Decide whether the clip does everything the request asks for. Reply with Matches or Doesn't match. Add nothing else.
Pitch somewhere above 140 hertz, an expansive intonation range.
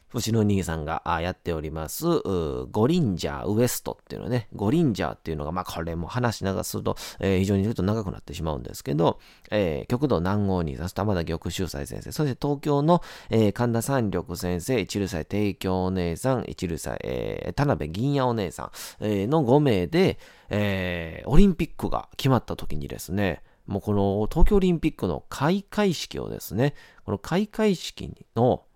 Doesn't match